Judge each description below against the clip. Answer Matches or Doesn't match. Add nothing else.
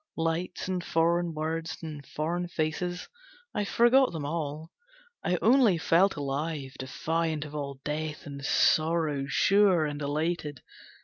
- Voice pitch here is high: Doesn't match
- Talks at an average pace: Doesn't match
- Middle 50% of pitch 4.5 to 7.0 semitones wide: Doesn't match